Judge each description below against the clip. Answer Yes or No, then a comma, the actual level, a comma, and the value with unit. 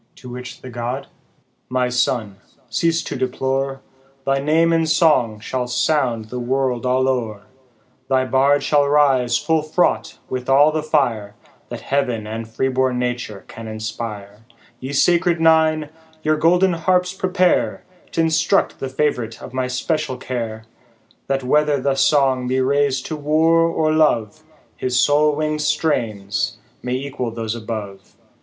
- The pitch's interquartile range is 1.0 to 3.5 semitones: No, average, 4.0 semitones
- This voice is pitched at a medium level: No, low, 130 Hz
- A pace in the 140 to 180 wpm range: Yes, average, 150 wpm